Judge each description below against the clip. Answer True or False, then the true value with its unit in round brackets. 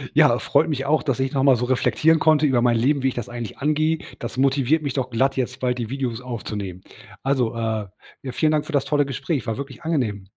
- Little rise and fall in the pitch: False (3.4 semitones)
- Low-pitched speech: True (130 Hz)